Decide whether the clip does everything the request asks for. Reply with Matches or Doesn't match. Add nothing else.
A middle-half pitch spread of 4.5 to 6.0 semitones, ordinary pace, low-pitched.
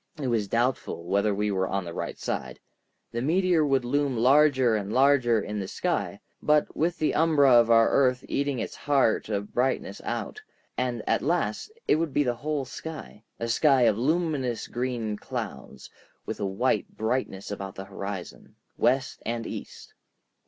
Matches